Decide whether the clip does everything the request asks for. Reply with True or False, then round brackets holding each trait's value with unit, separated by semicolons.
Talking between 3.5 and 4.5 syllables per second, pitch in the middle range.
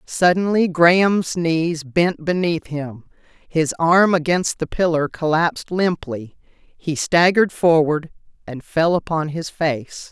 True (3.7 syllables/s; 165 Hz)